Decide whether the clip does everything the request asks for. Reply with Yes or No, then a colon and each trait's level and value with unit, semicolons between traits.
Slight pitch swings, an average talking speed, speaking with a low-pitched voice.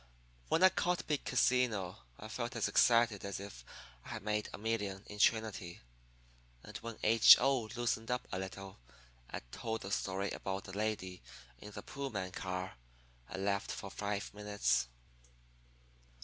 No: average, 3.2 semitones; average, 155 wpm; low, 105 Hz